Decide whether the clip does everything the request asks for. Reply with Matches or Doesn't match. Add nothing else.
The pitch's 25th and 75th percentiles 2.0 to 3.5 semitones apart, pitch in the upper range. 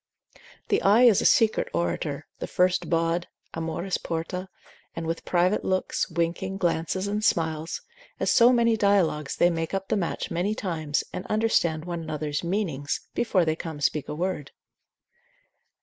Doesn't match